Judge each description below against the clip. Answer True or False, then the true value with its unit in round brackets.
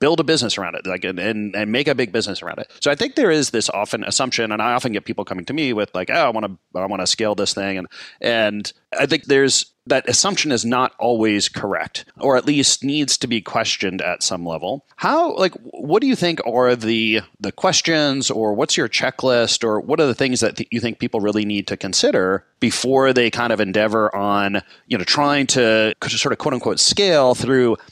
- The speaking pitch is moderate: False (115 Hz)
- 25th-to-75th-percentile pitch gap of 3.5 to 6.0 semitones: True (4.1 semitones)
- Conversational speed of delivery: False (230 wpm)